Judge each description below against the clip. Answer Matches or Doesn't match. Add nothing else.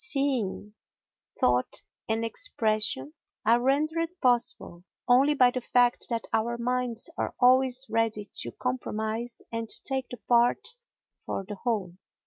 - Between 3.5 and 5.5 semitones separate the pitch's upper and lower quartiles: Doesn't match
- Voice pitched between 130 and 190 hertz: Doesn't match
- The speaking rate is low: Matches